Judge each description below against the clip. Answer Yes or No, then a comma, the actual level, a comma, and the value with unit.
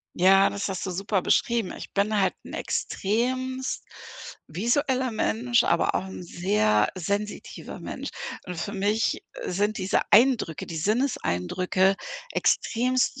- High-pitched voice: Yes, high, 200 Hz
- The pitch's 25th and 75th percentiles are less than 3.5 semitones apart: No, average, 4.4 semitones